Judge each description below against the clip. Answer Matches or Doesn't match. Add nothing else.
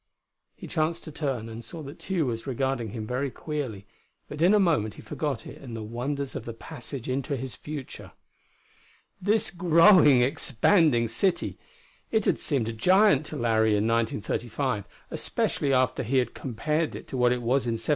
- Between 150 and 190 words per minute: Matches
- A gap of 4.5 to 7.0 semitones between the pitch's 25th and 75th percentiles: Matches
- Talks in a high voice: Doesn't match